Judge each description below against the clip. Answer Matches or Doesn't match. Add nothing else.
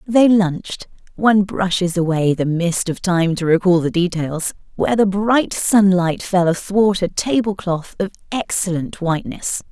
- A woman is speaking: Matches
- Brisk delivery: Doesn't match